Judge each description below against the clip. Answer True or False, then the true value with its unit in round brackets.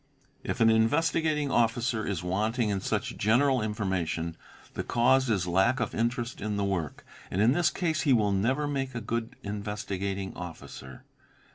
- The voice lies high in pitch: False (110 Hz)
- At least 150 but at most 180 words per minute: True (160 wpm)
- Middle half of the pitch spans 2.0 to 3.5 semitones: False (4.4 semitones)